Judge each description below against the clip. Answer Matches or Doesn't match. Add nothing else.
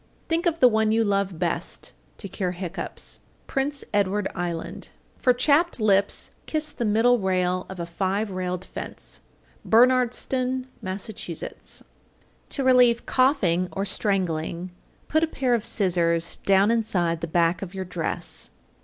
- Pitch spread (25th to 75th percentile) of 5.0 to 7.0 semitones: Matches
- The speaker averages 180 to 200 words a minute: Doesn't match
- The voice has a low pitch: Doesn't match